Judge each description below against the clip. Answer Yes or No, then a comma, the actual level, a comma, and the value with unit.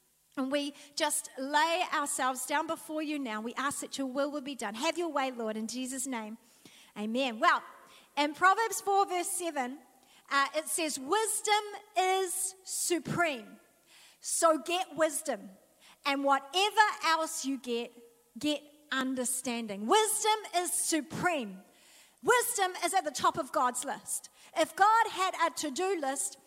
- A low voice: No, very high, 300 Hz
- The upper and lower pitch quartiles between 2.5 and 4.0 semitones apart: No, average, 5.2 semitones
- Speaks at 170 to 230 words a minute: No, average, 145 wpm